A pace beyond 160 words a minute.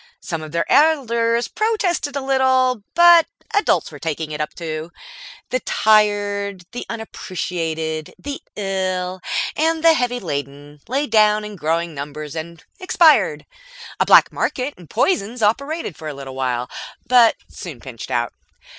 No: average, 145 wpm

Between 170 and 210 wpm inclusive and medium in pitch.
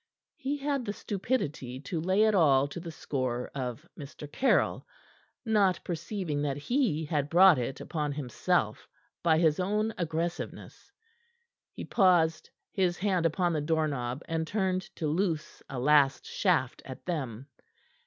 No: average, 145 wpm; medium, 160 Hz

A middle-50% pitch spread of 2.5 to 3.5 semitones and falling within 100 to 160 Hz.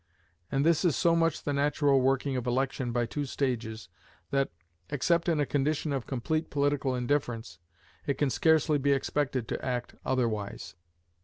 Yes: average, 2.9 semitones; low, 135 Hz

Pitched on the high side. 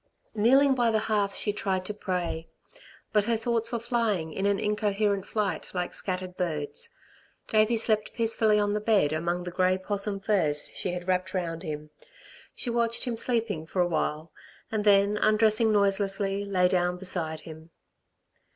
Yes: high, 200 Hz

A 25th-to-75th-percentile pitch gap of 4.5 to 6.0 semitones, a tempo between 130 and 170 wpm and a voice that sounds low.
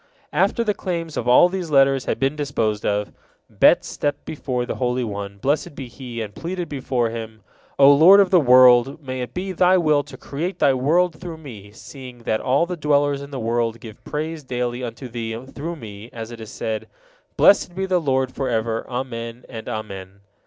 No: average, 4.8 semitones; average, 195 wpm; low, 130 Hz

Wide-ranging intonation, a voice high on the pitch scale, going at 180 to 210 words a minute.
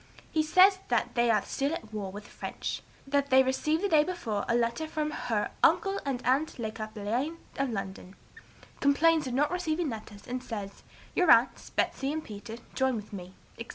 Yes: wide, 6.2 semitones; very high, 260 Hz; average, 190 wpm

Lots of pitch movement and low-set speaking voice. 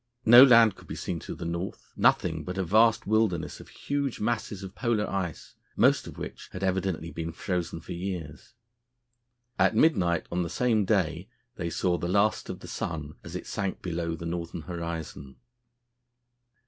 No: average, 3.9 semitones; very low, 90 Hz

